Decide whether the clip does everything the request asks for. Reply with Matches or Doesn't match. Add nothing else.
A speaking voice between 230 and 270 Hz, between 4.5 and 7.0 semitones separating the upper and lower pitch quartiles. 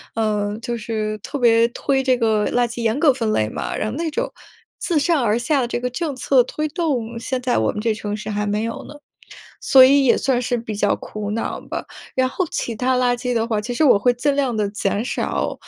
Doesn't match